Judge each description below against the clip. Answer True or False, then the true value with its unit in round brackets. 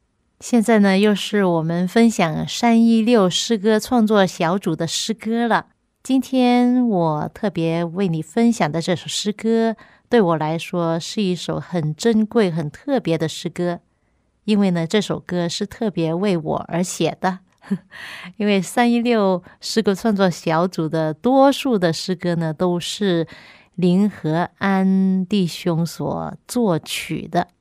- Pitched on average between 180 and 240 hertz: True (190 Hz)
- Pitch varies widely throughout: False (4.8 semitones)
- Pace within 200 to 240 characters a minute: True (205 characters per minute)